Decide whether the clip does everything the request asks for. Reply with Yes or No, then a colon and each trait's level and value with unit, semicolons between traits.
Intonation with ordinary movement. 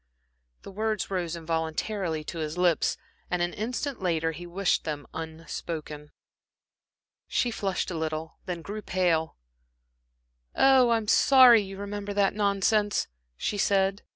Yes: average, 4.1 semitones